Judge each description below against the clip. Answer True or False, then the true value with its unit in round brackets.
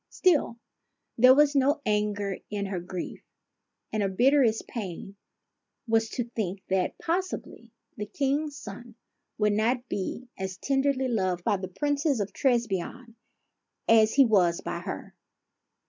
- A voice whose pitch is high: True (225 Hz)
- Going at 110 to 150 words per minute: True (135 wpm)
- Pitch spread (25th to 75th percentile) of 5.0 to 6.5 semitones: True (5.3 semitones)